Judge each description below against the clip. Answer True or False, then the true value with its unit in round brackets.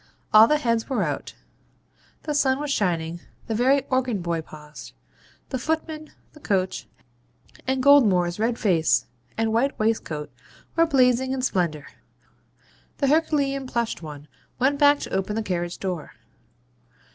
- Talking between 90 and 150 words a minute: True (140 wpm)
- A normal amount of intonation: False (7.4 semitones)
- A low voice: False (230 Hz)